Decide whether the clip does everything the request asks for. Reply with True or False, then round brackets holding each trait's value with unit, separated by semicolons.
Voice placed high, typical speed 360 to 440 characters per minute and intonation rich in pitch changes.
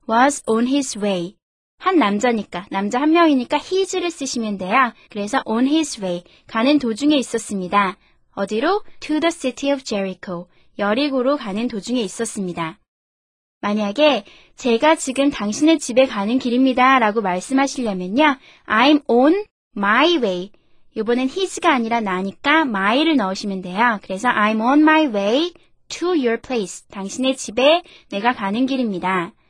True (245 Hz; 370 characters per minute; 6.0 semitones)